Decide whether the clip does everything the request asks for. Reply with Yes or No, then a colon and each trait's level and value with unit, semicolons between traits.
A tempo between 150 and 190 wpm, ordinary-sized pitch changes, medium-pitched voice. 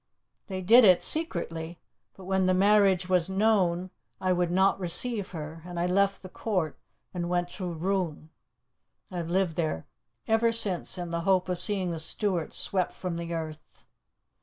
No: average, 165 wpm; narrow, 2.2 semitones; medium, 180 Hz